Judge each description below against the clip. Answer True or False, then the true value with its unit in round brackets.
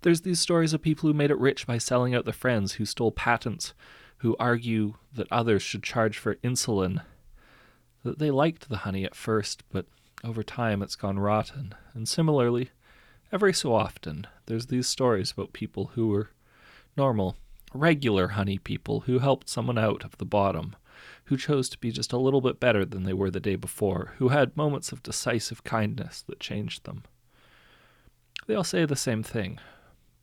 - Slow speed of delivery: False (180 wpm)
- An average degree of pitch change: True (4.5 semitones)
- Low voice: True (115 Hz)